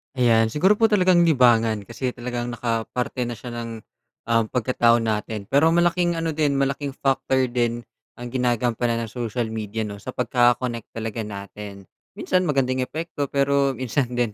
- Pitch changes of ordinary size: Yes, average, 3.2 semitones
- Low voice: Yes, low, 120 Hz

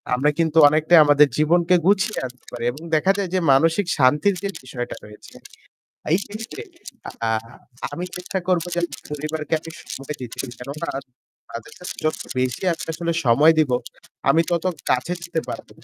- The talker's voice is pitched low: No, medium, 155 Hz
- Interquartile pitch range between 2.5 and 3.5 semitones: No, average, 4.2 semitones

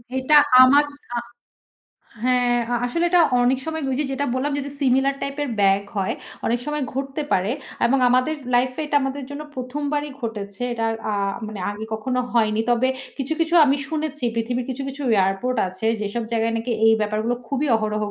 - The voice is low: No, very high, 255 Hz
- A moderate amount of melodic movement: Yes, average, 3.8 semitones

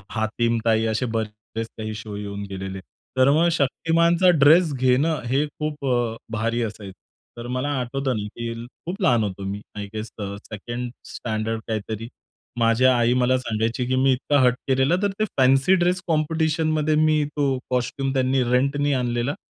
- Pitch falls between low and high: No, low, 125 Hz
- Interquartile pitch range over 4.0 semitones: Yes, average, 4.4 semitones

